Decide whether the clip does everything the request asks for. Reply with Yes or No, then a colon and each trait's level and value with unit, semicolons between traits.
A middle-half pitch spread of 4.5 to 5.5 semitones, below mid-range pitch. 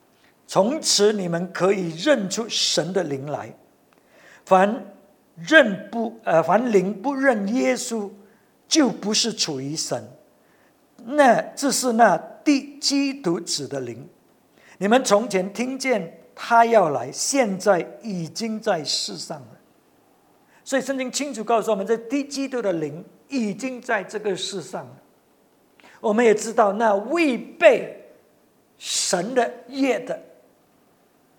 No: average, 5.0 semitones; high, 220 Hz